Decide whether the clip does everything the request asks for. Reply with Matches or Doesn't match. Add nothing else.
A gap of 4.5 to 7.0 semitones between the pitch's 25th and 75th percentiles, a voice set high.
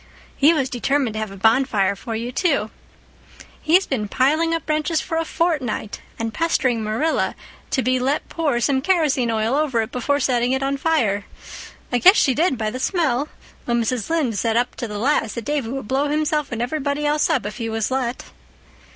Matches